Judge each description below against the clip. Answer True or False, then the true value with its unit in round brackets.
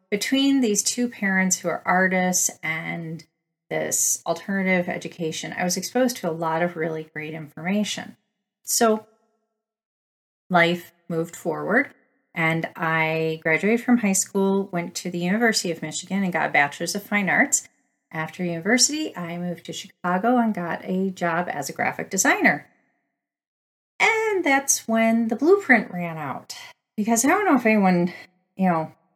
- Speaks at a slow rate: False (150 wpm)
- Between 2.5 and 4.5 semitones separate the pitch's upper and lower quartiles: False (5.0 semitones)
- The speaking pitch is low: False (185 Hz)